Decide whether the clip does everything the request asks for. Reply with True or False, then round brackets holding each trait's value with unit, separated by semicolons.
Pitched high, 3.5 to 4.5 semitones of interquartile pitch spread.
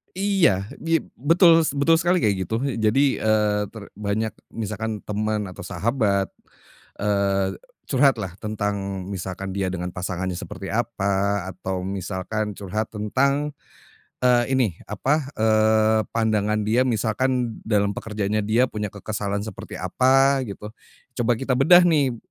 False (110 Hz; 4.2 semitones)